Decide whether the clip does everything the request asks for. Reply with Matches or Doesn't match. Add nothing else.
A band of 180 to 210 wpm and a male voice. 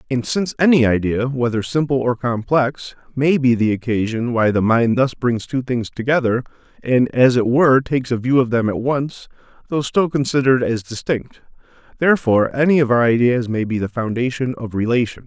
Matches